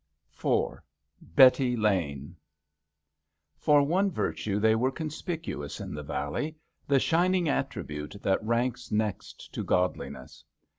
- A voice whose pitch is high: No, low, 120 Hz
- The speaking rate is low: Yes, slow, 130 wpm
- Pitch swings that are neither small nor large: No, wide, 7.7 semitones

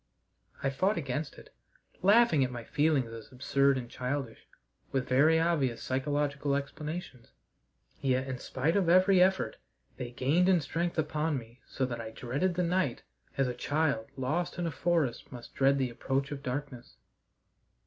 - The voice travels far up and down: No, average, 4.2 semitones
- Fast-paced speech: No, average, 160 wpm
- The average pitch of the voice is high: No, medium, 140 Hz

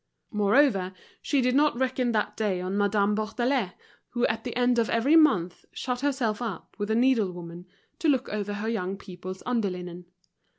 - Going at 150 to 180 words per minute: Yes, average, 175 wpm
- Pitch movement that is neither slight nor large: Yes, average, 4.6 semitones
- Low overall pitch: No, high, 220 Hz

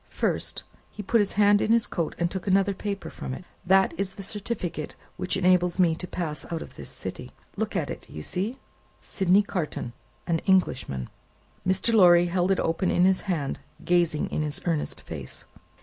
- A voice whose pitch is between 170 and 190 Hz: Yes, medium, 185 Hz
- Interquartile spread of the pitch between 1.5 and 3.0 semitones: Yes, narrow, 2.5 semitones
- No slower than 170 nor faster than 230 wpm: Yes, average, 185 wpm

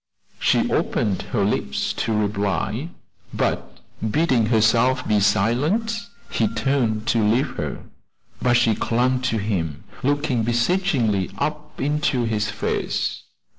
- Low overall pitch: Yes, low, 115 Hz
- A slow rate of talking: Yes, slow, 120 wpm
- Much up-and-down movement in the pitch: No, average, 4.3 semitones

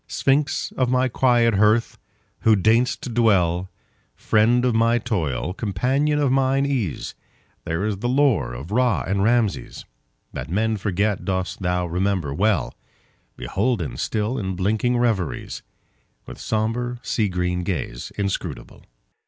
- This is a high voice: No, low, 110 Hz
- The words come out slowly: Yes, slow, 120 wpm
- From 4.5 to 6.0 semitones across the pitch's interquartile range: Yes, average, 4.9 semitones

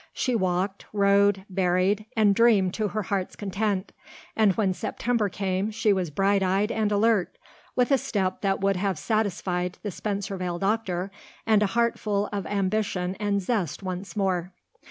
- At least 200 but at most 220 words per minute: No, average, 160 wpm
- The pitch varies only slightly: Yes, narrow, 2.2 semitones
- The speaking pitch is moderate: No, high, 200 Hz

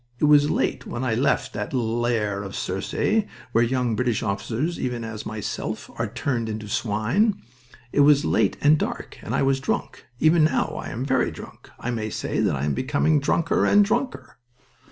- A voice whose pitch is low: Yes, low, 125 Hz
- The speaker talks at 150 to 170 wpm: No, average, 185 wpm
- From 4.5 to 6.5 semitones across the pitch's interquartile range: Yes, average, 5.1 semitones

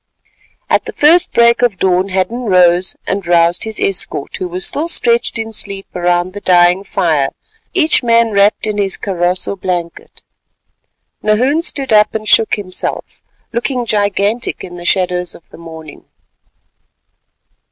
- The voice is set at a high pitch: Yes, high, 195 Hz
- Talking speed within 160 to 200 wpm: No, average, 150 wpm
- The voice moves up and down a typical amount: Yes, average, 4.2 semitones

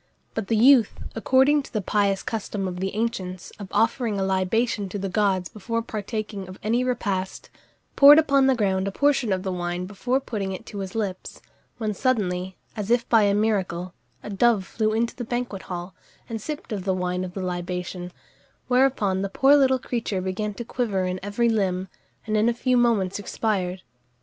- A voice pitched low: No, high, 205 Hz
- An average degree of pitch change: Yes, average, 3.8 semitones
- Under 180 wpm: No, average, 190 wpm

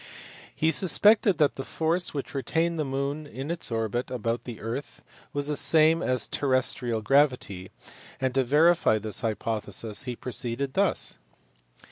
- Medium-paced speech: Yes, average, 145 wpm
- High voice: No, low, 135 Hz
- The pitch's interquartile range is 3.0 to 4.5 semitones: No, average, 4.9 semitones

